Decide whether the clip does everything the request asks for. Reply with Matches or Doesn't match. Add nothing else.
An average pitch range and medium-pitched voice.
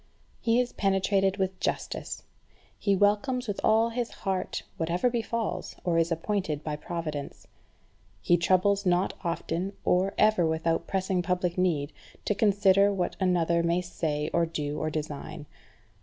Matches